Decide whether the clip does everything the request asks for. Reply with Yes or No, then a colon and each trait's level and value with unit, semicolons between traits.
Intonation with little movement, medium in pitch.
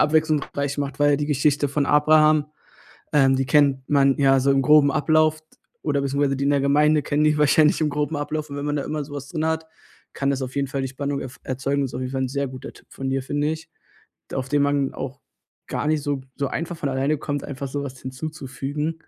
Yes: narrow, 1.8 semitones; medium, 145 Hz